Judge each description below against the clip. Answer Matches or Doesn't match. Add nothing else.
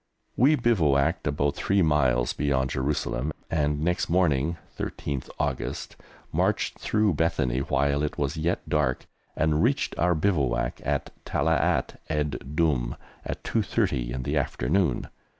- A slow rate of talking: Matches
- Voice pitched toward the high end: Doesn't match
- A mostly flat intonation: Doesn't match